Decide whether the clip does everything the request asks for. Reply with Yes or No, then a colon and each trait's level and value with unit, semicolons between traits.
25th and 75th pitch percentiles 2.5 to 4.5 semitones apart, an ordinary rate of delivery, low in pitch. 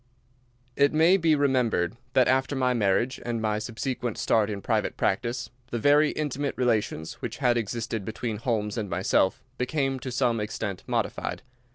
Yes: average, 3.6 semitones; average, 160 wpm; low, 120 Hz